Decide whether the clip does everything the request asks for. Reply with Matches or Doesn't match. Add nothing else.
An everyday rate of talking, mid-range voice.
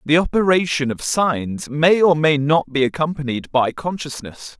Matches